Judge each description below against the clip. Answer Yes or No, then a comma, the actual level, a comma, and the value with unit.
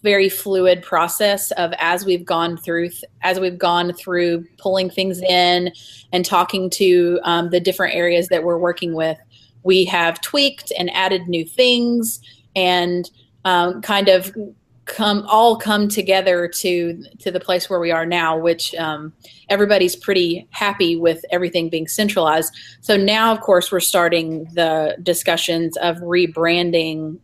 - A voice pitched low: No, medium, 175 Hz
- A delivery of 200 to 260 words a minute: No, average, 150 wpm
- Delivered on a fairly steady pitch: Yes, narrow, 2.1 semitones